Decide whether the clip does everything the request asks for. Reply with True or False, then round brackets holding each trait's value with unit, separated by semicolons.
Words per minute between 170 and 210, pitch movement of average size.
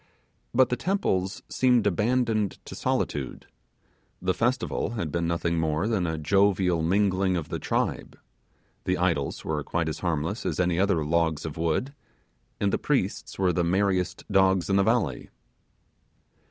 False (155 wpm; 3.5 semitones)